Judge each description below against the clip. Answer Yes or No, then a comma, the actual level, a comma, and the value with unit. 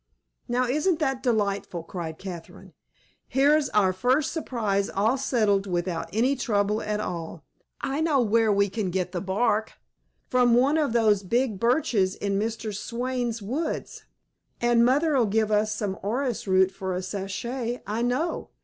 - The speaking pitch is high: Yes, high, 220 Hz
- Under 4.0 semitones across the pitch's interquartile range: No, average, 4.3 semitones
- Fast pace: No, average, 150 wpm